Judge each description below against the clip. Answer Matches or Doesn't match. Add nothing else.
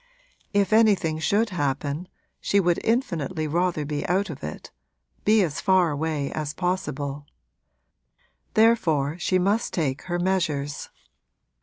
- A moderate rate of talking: Doesn't match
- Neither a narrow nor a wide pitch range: Matches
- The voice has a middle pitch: Matches